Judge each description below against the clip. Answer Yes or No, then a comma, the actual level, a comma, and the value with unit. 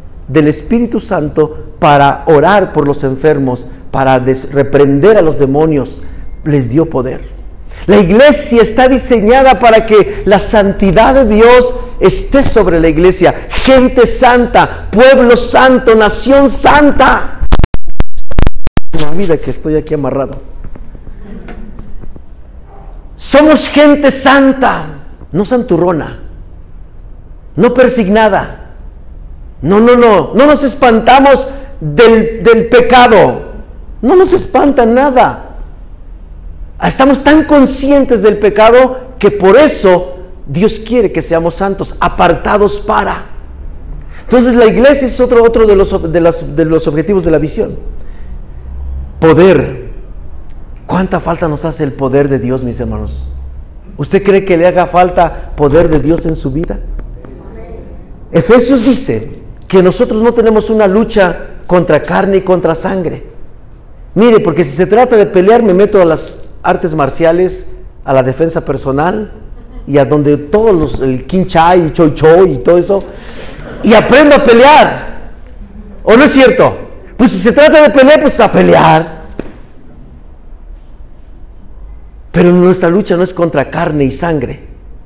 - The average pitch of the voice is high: No, medium, 180 Hz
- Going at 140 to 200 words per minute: No, average, 130 wpm